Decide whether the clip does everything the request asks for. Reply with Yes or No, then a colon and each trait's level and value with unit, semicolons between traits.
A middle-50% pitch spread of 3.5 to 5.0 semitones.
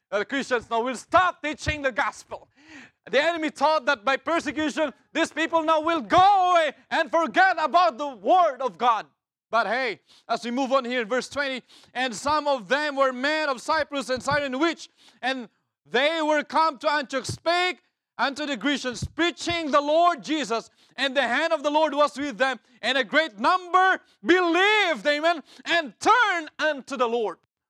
Yes: average, 3.8 semitones